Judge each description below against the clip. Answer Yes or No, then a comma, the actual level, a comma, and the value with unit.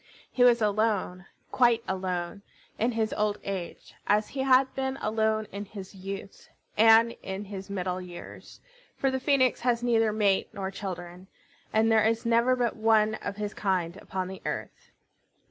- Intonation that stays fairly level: No, average, 3.3 semitones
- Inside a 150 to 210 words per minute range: Yes, average, 160 wpm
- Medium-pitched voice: No, high, 215 Hz